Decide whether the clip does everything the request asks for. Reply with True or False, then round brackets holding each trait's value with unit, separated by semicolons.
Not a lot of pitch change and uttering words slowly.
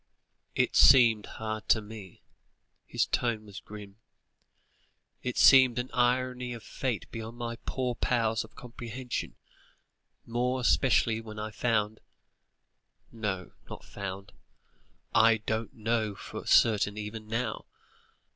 True (2.3 semitones; 120 wpm)